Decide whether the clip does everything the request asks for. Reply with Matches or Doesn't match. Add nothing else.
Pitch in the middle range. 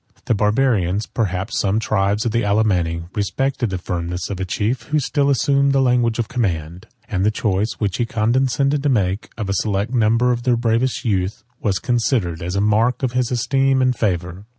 Doesn't match